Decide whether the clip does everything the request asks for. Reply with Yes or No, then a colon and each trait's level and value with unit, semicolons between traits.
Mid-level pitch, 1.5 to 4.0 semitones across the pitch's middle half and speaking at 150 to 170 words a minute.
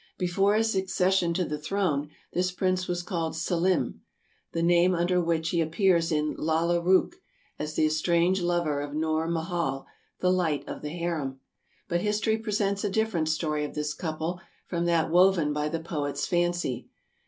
No: medium, 170 Hz; average, 2.8 semitones; average, 180 wpm